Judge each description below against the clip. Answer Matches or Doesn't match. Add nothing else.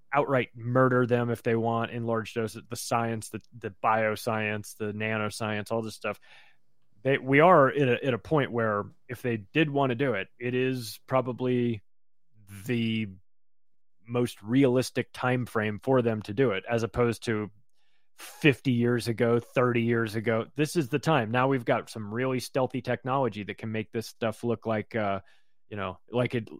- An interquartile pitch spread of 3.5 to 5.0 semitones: Doesn't match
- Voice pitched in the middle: Doesn't match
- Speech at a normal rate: Matches